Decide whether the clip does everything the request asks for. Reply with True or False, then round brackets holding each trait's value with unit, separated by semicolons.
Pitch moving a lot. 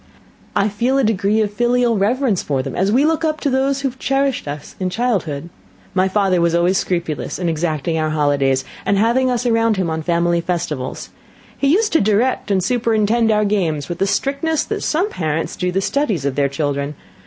True (6.7 semitones)